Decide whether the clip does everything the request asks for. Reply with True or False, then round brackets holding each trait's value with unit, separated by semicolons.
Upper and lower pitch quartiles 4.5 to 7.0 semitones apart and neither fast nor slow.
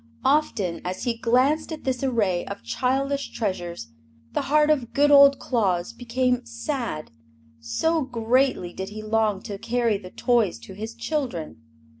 True (5.4 semitones; 150 wpm)